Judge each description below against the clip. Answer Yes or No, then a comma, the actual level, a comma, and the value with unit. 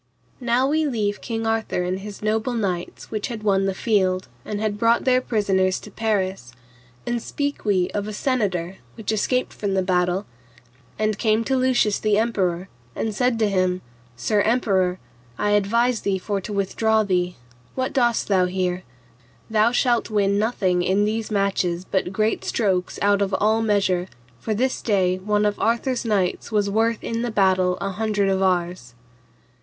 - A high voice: Yes, high, 205 Hz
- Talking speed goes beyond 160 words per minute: Yes, average, 170 wpm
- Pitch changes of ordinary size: Yes, average, 3.0 semitones